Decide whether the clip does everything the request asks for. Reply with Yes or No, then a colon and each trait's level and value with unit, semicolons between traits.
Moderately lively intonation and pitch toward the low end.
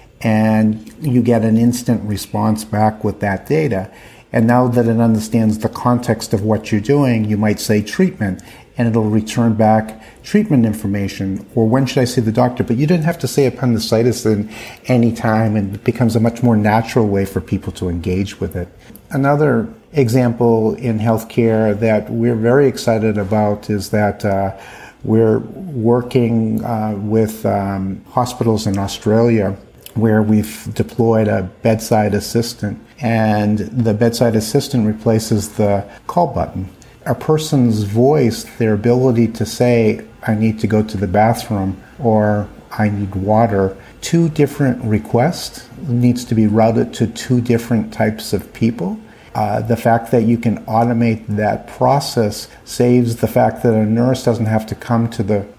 No: narrow, 2.1 semitones; low, 110 Hz